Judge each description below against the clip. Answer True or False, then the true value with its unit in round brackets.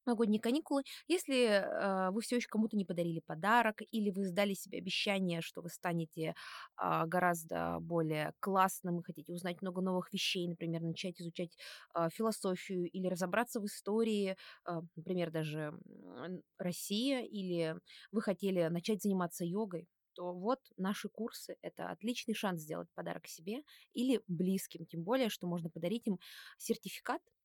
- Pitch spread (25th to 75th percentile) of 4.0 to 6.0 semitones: True (4.3 semitones)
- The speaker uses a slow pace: False (145 wpm)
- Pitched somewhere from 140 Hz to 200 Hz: True (190 Hz)